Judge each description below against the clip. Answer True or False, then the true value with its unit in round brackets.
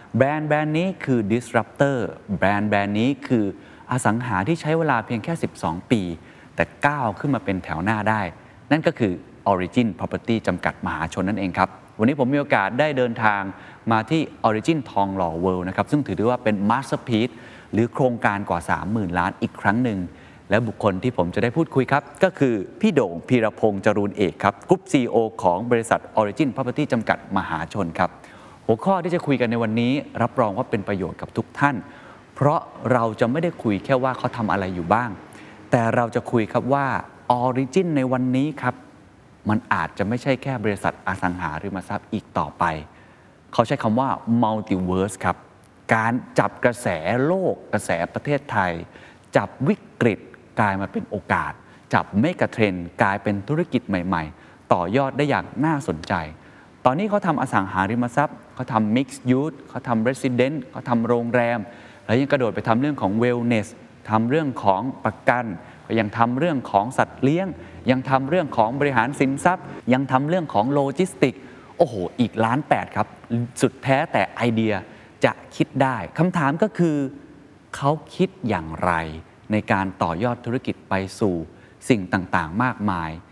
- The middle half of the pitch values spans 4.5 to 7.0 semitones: True (5.2 semitones)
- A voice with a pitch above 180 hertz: False (120 Hz)